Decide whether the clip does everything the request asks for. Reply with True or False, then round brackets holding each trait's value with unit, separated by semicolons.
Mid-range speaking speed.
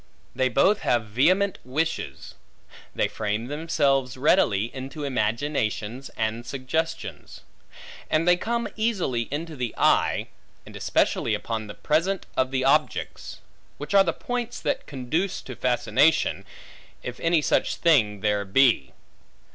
False (125 wpm)